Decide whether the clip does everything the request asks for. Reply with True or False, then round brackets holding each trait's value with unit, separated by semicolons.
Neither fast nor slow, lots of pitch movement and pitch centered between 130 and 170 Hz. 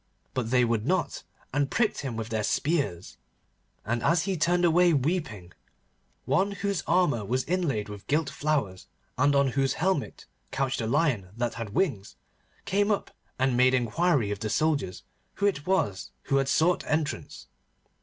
True (165 wpm; 6.8 semitones; 140 Hz)